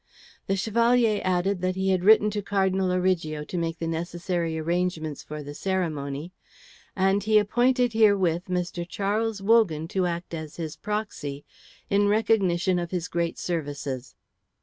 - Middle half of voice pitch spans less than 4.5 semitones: Yes, average, 3.6 semitones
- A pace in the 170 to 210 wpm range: No, average, 150 wpm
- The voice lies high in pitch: No, medium, 180 Hz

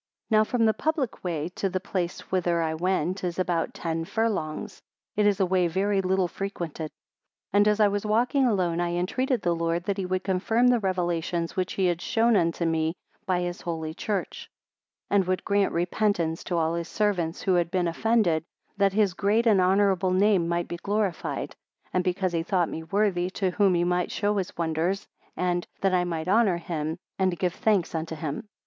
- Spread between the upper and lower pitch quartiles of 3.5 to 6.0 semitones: No, average, 2.9 semitones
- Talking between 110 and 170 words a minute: No, average, 200 wpm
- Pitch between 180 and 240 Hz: Yes, medium, 185 Hz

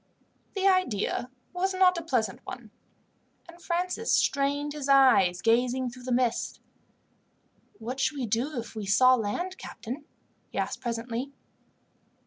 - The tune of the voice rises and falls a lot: Yes, wide, 5.8 semitones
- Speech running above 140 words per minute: No, slow, 135 wpm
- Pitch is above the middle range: Yes, very high, 255 Hz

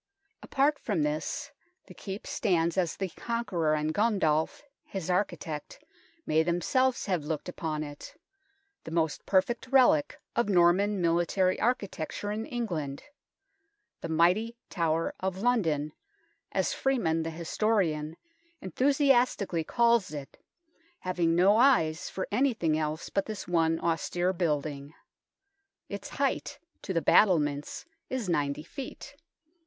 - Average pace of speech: No, slow, 125 wpm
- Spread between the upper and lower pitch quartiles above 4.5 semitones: Yes, wide, 5.4 semitones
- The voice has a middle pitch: Yes, medium, 175 Hz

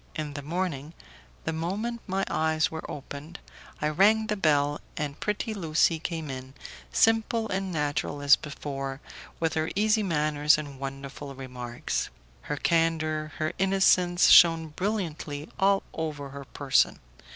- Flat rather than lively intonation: No, average, 4.2 semitones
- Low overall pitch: No, medium, 155 Hz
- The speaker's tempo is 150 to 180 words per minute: No, average, 140 wpm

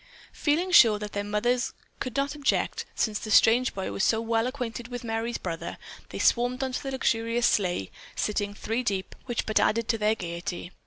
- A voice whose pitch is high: Yes, high, 225 Hz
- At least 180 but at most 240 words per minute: Yes, average, 190 wpm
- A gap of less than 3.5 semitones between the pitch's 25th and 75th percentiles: Yes, average, 2.9 semitones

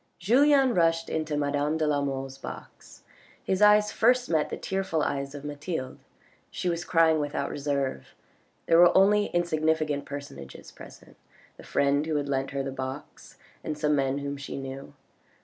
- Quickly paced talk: No, average, 160 wpm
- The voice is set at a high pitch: No, medium, 150 Hz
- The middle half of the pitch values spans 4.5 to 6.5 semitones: No, average, 3.5 semitones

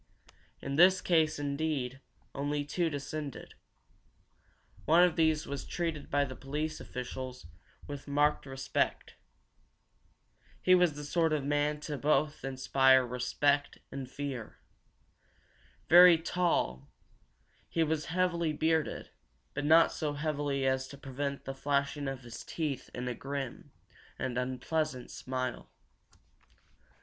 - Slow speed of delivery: Yes, slow, 120 wpm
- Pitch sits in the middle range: Yes, medium, 145 Hz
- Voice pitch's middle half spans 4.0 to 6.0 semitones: No, average, 2.9 semitones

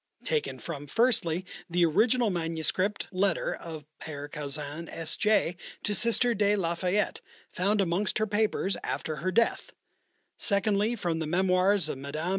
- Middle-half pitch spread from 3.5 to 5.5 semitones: Yes, average, 4.2 semitones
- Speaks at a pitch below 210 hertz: Yes, medium, 185 Hz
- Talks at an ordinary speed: Yes, average, 145 wpm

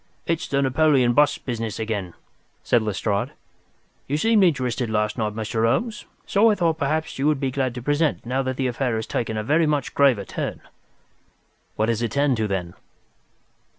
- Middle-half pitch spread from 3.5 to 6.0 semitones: Yes, average, 4.8 semitones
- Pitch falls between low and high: No, low, 130 Hz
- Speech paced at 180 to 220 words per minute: Yes, average, 185 wpm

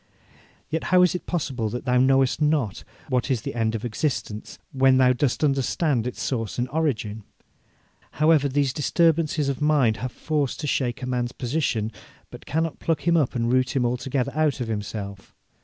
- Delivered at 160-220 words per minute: Yes, average, 180 wpm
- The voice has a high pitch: No, low, 130 Hz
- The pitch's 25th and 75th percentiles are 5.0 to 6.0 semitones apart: No, average, 3.8 semitones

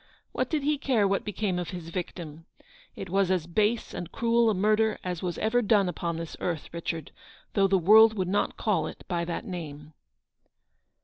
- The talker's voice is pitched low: No, high, 190 Hz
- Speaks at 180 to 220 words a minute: Yes, average, 190 wpm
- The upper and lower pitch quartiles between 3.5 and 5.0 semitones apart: Yes, average, 4.1 semitones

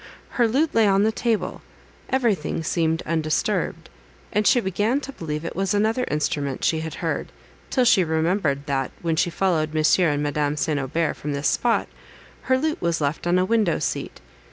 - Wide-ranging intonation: Yes, wide, 6.1 semitones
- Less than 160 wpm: No, average, 180 wpm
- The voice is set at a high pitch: No, medium, 170 Hz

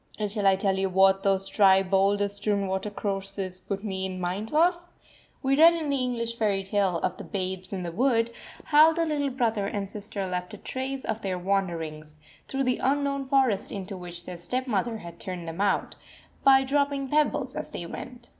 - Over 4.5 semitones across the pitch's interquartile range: Yes, wide, 5.5 semitones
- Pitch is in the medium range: No, high, 200 Hz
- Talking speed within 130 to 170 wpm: No, average, 190 wpm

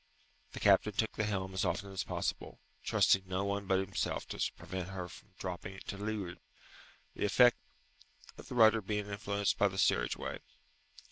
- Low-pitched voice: Yes, low, 100 Hz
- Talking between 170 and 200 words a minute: Yes, average, 175 wpm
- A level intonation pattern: Yes, narrow, 1.8 semitones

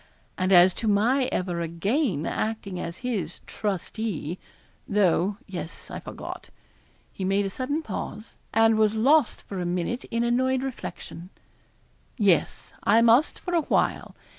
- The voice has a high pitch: Yes, high, 210 Hz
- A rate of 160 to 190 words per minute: No, average, 140 wpm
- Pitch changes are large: No, average, 4.6 semitones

